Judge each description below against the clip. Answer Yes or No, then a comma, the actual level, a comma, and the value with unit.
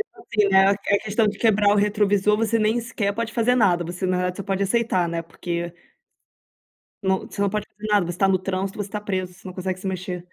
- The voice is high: Yes, high, 200 Hz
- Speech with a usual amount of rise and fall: No, narrow, 2.2 semitones